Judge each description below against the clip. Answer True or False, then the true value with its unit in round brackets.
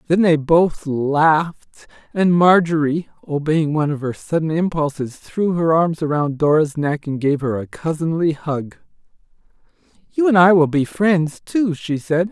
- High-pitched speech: False (160 Hz)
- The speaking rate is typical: True (160 wpm)